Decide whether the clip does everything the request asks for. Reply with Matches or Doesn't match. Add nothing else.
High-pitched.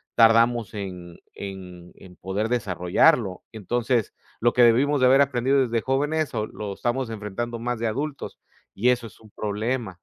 Doesn't match